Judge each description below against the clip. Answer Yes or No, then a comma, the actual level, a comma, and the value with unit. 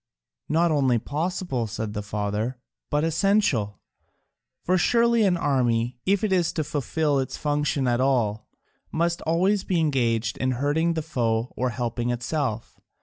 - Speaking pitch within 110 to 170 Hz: Yes, medium, 140 Hz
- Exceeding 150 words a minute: No, average, 145 wpm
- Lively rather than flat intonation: Yes, wide, 5.9 semitones